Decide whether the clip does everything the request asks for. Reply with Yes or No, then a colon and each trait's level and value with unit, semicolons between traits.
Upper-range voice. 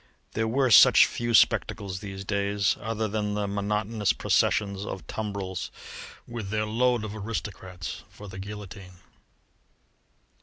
No: low, 105 Hz